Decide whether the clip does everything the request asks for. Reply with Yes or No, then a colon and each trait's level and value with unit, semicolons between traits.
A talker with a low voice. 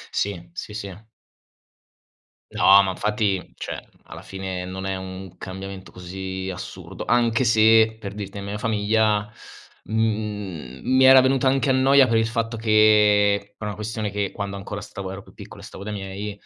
Yes: low, 105 Hz